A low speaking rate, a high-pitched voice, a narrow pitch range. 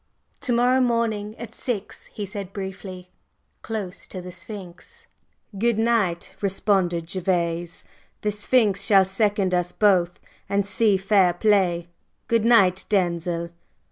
No: slow, 120 wpm; high, 195 Hz; average, 3.0 semitones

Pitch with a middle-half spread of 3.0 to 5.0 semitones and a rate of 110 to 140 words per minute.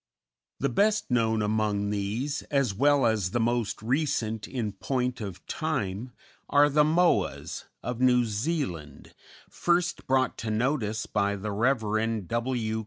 Yes: average, 4.4 semitones; slow, 135 wpm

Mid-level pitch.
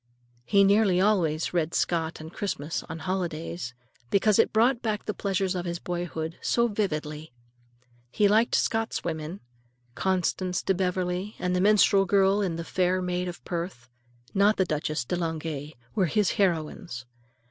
Yes: medium, 180 Hz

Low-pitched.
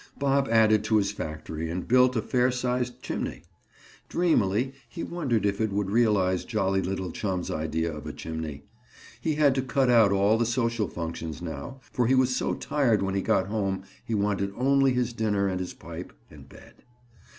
Yes: low, 110 Hz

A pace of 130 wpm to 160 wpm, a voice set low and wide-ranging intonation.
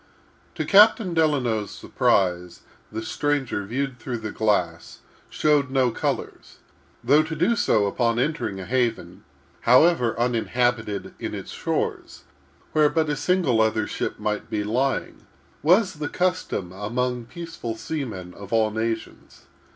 Yes: slow, 135 wpm; low, 120 Hz; wide, 5.7 semitones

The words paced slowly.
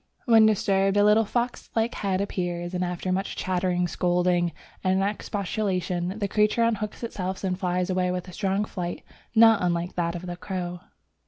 No: average, 170 wpm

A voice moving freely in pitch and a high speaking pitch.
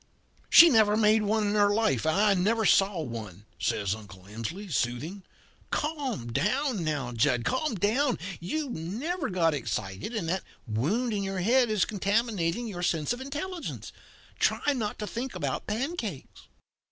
Yes: wide, 7.4 semitones; high, 205 Hz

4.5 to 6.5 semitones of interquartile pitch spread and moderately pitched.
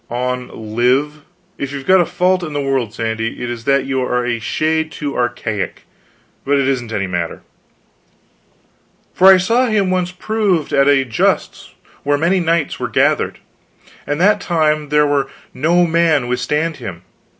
Yes: wide, 5.4 semitones; medium, 145 Hz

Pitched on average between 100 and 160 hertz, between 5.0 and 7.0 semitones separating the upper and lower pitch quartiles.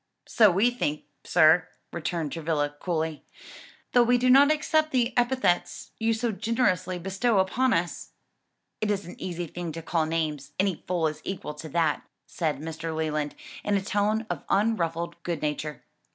No: medium, 175 Hz; wide, 5.6 semitones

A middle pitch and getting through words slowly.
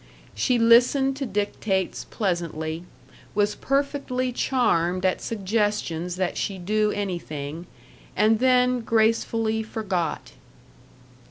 No: high, 210 Hz; slow, 95 wpm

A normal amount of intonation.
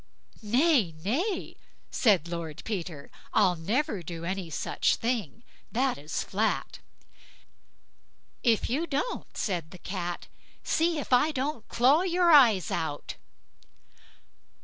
No: wide, 8.6 semitones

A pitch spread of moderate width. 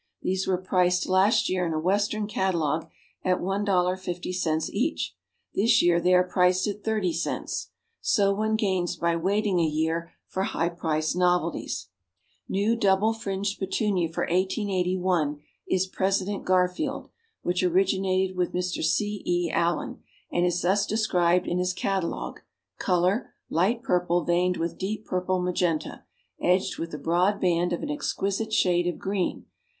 No: narrow, 2.1 semitones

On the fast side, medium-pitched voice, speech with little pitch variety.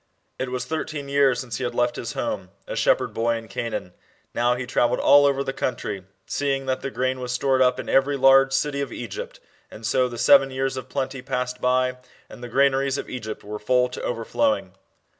No: fast, 215 wpm; low, 130 Hz; narrow, 1.8 semitones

